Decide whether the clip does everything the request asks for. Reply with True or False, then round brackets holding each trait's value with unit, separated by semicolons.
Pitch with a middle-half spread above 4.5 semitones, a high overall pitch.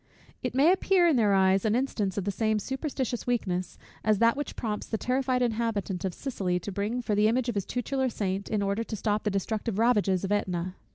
False (3.9 semitones; 215 Hz)